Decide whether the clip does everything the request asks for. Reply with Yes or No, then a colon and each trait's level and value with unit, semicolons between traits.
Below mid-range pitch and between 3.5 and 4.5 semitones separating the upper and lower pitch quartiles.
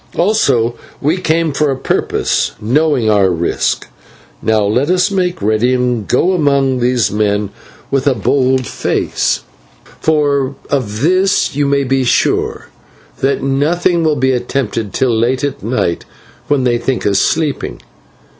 Yes: low, 130 Hz; average, 4.1 semitones